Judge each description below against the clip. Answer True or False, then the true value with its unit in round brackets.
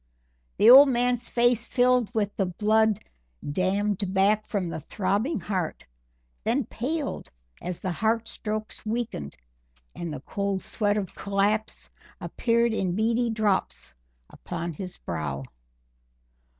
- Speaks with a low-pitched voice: False (210 Hz)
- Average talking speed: False (125 wpm)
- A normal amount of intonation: True (3.7 semitones)